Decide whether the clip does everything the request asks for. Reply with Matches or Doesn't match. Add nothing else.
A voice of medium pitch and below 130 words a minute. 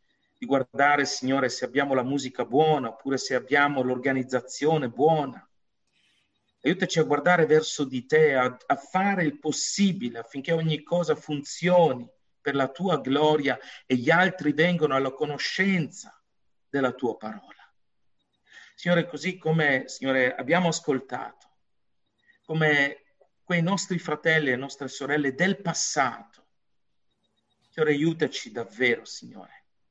Matches